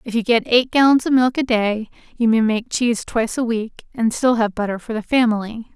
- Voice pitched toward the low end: No, high, 230 Hz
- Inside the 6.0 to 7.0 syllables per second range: No, 5.5 syllables/s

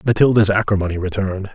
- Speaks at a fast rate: No, slow, 115 wpm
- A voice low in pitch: Yes, low, 100 Hz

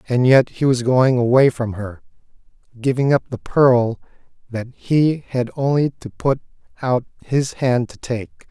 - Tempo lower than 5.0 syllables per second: Yes, 4.1 syllables/s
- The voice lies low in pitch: Yes, low, 125 Hz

